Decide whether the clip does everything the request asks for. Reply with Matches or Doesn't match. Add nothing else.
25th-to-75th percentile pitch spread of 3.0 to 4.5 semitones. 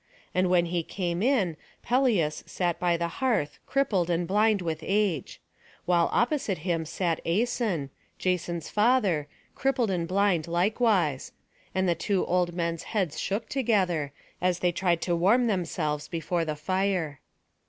Matches